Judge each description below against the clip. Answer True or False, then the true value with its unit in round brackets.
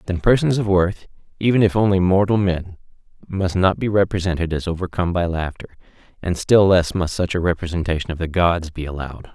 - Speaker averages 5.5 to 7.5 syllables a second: True (5.8 syllables/s)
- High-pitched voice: False (90 Hz)